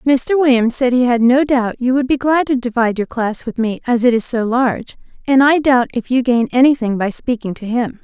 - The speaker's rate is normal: No, fast, 245 wpm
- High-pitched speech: Yes, very high, 250 Hz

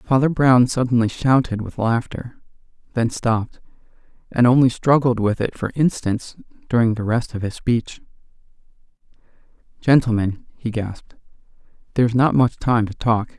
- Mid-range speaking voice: No, low, 120 Hz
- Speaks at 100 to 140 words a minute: Yes, slow, 135 wpm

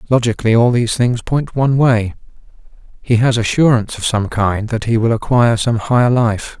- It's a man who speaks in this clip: Yes, male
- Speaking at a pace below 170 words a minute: No, average, 180 wpm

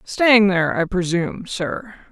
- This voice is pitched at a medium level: No, high, 195 Hz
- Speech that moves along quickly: No, average, 140 wpm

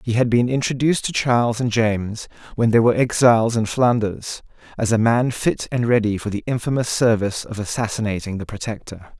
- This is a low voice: Yes, low, 115 Hz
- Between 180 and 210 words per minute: Yes, average, 185 wpm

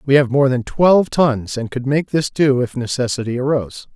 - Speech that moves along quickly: Yes, fast, 210 wpm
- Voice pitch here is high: No, low, 135 Hz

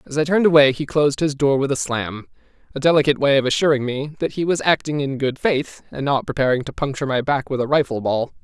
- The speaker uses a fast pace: Yes, fast, 240 wpm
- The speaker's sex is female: No, male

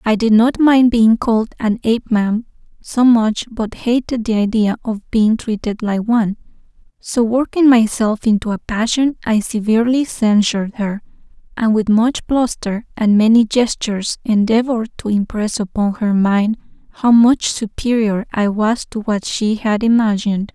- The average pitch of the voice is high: Yes, high, 220 Hz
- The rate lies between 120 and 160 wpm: Yes, average, 150 wpm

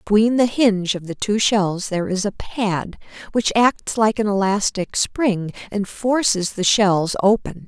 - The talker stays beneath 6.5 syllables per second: Yes, 4.1 syllables/s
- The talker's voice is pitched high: Yes, high, 205 Hz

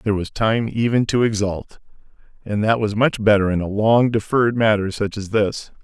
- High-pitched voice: No, low, 105 Hz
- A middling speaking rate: Yes, average, 195 wpm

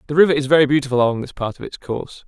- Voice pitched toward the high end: No, medium, 140 Hz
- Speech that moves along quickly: Yes, fast, 290 wpm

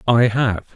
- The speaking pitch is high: No, low, 115 Hz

